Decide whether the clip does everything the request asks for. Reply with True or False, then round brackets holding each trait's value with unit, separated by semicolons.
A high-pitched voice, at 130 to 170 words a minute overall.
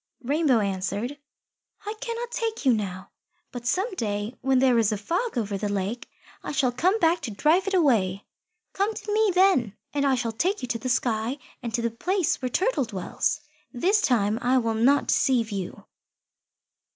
False (250 Hz; 185 wpm)